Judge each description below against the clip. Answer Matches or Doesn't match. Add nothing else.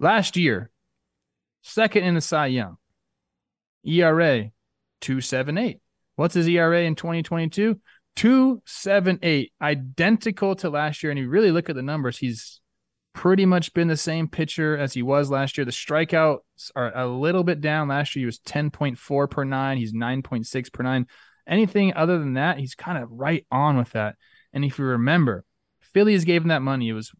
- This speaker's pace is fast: Doesn't match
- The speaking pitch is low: Doesn't match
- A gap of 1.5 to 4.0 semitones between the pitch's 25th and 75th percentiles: Doesn't match